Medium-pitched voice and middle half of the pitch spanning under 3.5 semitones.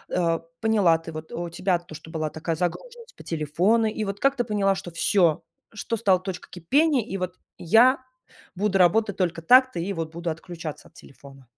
No: medium, 180 Hz; average, 4.8 semitones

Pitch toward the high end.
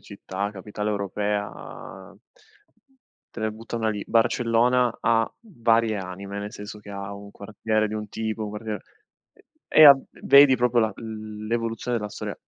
No: low, 110 Hz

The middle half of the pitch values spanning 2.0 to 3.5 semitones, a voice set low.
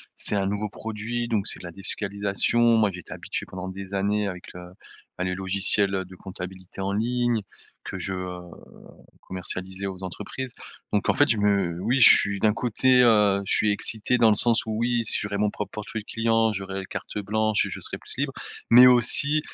Yes: average, 2.9 semitones; low, 105 Hz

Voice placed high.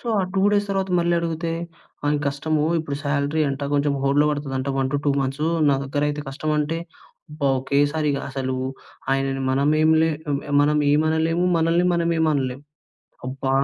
No: medium, 150 Hz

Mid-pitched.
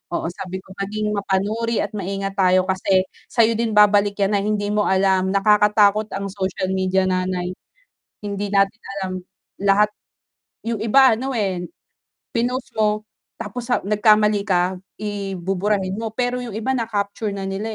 No: high, 205 Hz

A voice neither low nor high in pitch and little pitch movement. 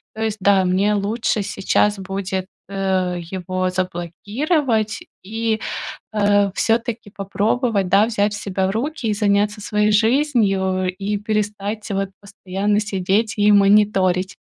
No: high, 205 Hz; narrow, 2.0 semitones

